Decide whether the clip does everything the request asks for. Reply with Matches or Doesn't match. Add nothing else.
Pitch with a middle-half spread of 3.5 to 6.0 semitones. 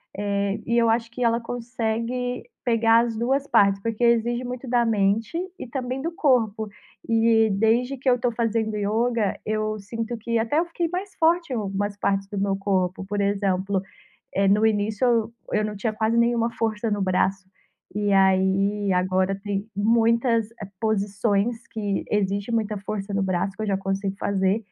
Doesn't match